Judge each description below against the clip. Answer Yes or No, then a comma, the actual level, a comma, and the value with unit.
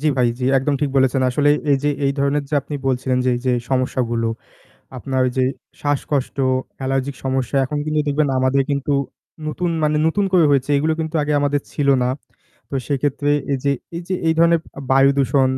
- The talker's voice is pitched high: No, medium, 140 Hz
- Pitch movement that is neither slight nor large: No, narrow, 2.0 semitones